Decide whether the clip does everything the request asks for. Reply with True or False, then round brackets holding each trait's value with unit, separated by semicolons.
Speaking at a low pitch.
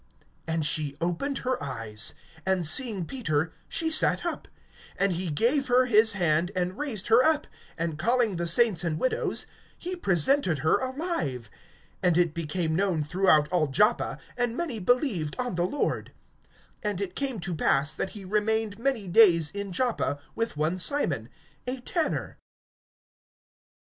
False (190 Hz)